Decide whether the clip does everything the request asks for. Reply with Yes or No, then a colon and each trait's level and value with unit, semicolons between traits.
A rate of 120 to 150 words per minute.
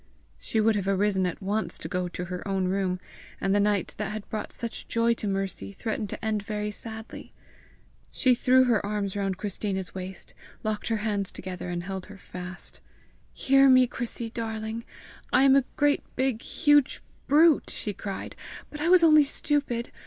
No: average, 180 wpm